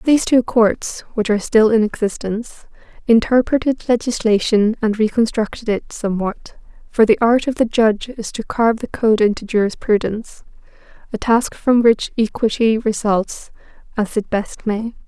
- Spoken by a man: No, female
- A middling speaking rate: Yes, average, 145 wpm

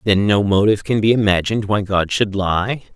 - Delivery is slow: No, fast, 205 wpm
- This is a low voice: Yes, low, 100 Hz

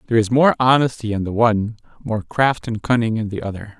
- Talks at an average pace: No, fast, 220 wpm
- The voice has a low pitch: Yes, low, 115 Hz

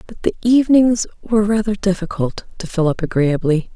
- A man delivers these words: No, female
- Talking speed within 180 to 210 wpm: No, average, 160 wpm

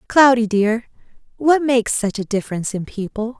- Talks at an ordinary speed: Yes, average, 160 wpm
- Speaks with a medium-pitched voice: No, high, 230 Hz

